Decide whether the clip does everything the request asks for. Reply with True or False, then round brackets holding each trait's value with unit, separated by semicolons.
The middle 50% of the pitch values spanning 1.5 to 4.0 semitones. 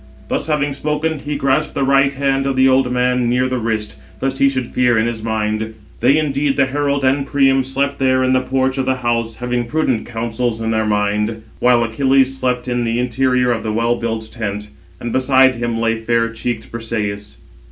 True (2.9 semitones)